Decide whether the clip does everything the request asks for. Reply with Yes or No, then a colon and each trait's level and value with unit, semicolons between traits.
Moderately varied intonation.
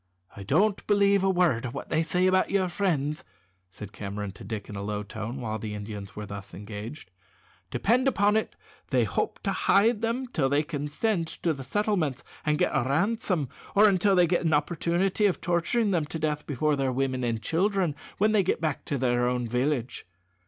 No: wide, 7.8 semitones